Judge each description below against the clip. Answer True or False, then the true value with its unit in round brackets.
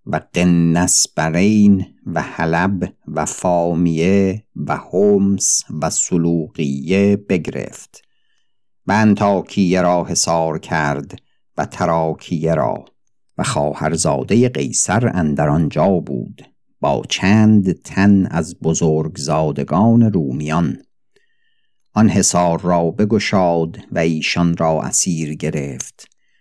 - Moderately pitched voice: False (85 Hz)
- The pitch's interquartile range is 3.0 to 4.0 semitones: True (3.7 semitones)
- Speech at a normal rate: False (95 wpm)